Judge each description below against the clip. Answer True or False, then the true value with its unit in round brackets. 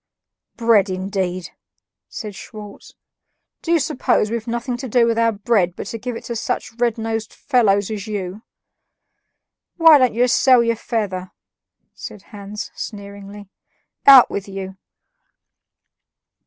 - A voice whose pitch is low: False (215 Hz)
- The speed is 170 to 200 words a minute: False (135 wpm)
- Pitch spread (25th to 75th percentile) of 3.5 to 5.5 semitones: False (2.9 semitones)